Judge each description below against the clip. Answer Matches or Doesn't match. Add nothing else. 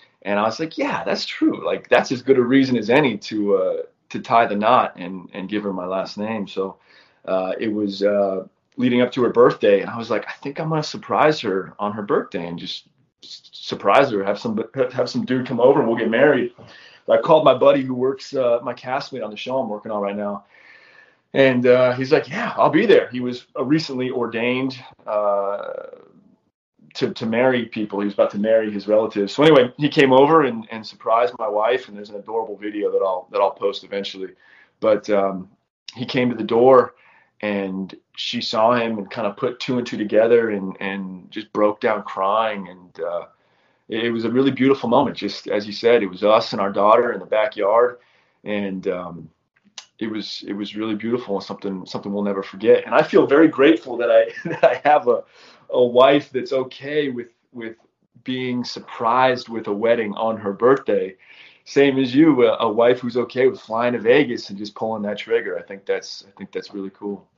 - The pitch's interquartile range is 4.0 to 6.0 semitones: Matches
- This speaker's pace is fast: Matches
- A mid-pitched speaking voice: Doesn't match